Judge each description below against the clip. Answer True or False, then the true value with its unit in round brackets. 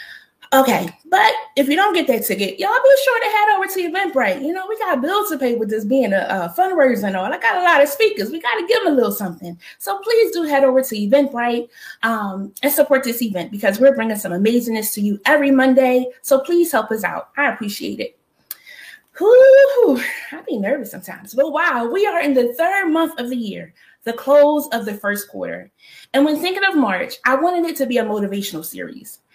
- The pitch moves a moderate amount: False (7.3 semitones)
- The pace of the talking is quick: True (225 wpm)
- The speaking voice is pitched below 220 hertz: False (275 Hz)